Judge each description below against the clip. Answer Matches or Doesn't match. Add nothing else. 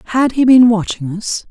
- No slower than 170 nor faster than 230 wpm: Matches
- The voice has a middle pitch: Doesn't match